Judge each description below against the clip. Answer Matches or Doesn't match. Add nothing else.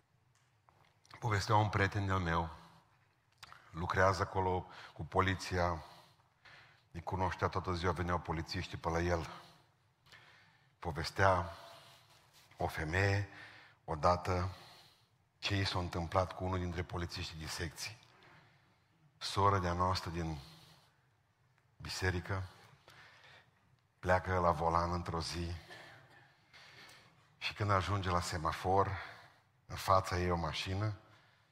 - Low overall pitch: Matches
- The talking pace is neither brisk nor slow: Doesn't match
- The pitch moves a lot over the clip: Doesn't match